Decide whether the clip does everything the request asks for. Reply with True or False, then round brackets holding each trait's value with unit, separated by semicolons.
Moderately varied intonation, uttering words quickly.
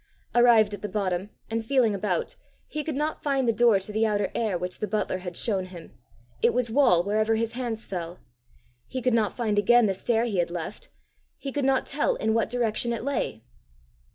True (3.6 semitones; 210 wpm)